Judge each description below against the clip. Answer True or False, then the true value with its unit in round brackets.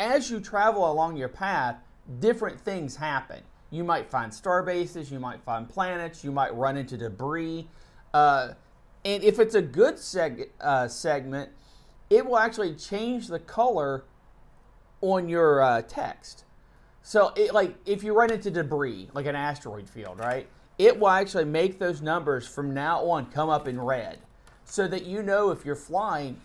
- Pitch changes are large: True (6.7 semitones)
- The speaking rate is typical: True (170 wpm)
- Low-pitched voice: False (165 Hz)